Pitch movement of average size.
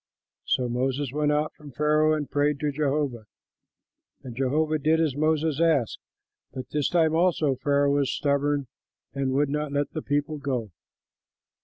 No: narrow, 2.0 semitones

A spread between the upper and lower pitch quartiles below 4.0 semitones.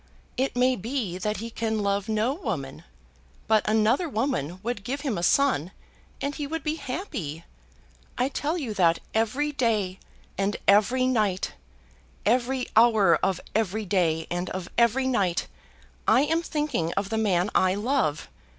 No: wide, 5.4 semitones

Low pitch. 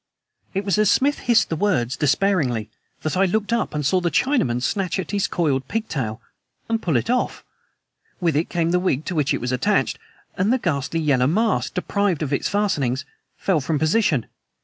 No: medium, 170 Hz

